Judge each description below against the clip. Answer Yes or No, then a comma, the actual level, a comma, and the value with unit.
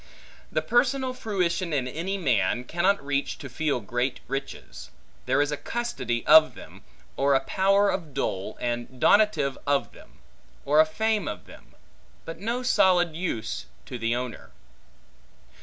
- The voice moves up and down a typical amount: No, wide, 7.4 semitones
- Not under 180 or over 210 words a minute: No, average, 150 wpm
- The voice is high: No, medium, 150 Hz